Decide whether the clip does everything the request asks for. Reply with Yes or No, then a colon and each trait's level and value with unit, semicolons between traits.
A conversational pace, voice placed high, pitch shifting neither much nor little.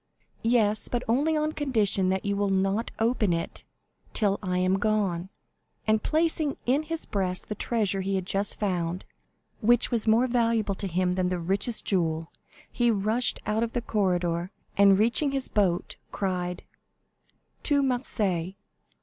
Yes: average, 155 wpm; high, 205 Hz; average, 4.2 semitones